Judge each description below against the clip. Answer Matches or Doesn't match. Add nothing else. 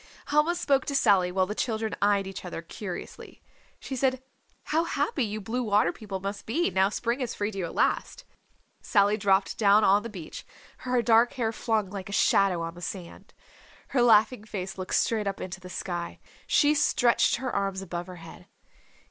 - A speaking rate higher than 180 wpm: Matches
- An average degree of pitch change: Matches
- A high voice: Matches